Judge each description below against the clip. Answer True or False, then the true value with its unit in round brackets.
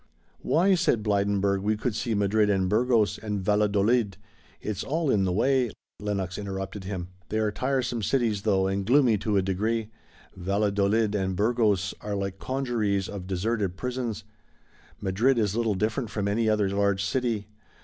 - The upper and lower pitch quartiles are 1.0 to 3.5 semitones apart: True (2.8 semitones)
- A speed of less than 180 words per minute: True (160 wpm)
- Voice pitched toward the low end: True (105 Hz)